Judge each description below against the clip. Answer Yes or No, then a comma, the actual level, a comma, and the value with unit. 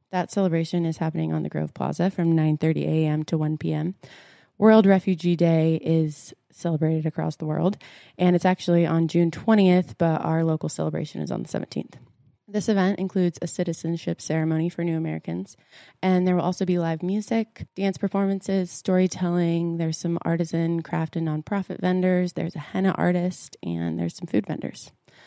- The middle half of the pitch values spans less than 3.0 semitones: Yes, narrow, 2.5 semitones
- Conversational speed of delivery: Yes, average, 170 wpm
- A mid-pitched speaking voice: Yes, medium, 170 Hz